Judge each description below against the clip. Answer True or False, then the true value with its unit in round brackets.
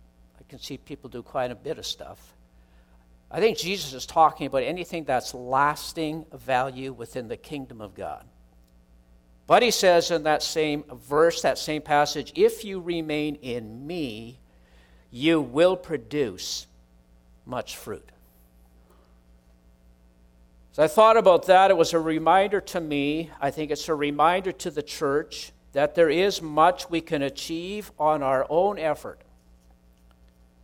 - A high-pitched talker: False (140 Hz)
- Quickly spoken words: False (145 wpm)